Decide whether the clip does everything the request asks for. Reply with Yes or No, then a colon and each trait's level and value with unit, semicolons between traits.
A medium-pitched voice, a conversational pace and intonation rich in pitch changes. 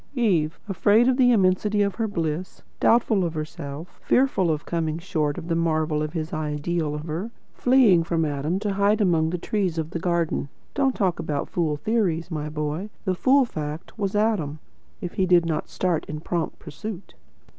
No: medium, 170 Hz; average, 185 wpm; average, 4.6 semitones